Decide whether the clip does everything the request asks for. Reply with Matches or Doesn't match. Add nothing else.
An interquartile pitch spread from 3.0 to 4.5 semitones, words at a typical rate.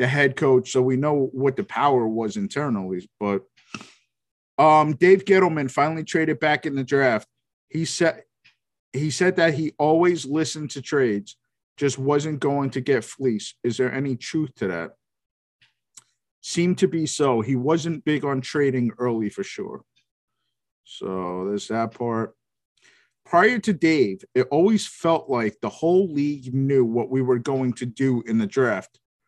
Matches